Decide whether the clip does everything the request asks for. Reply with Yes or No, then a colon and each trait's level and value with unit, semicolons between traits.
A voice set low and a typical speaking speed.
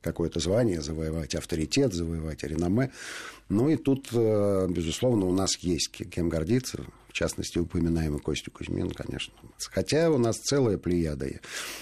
Yes: very low, 90 Hz; average, 130 wpm